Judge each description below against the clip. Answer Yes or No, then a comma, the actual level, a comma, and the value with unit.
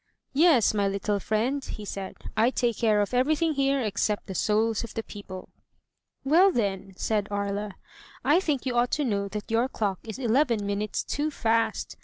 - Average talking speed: Yes, average, 185 wpm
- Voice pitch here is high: Yes, high, 220 Hz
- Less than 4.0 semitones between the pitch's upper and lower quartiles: No, average, 4.5 semitones